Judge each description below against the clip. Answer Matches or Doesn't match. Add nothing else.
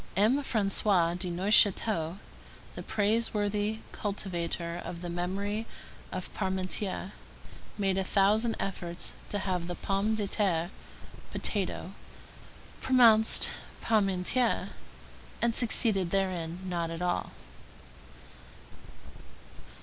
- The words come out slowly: Matches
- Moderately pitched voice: Doesn't match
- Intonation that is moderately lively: Matches